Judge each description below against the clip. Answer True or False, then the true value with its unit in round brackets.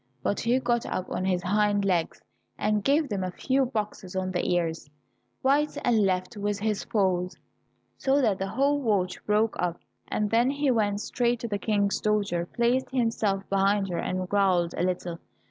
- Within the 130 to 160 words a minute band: False (180 wpm)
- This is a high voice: True (205 Hz)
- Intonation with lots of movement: False (4.2 semitones)